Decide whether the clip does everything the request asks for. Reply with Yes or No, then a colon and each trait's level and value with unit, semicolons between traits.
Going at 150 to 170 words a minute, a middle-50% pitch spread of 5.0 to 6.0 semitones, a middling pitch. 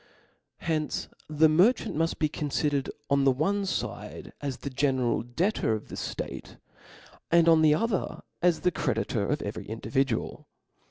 No: average, 155 wpm; average, 3.8 semitones; medium, 150 Hz